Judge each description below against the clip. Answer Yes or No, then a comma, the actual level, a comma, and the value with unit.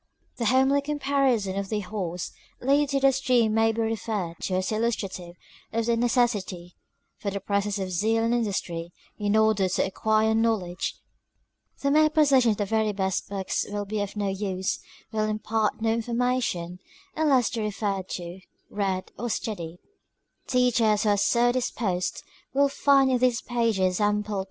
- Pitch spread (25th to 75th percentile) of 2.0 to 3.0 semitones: No, average, 3.8 semitones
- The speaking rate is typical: Yes, average, 170 wpm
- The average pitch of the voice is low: No, high, 215 Hz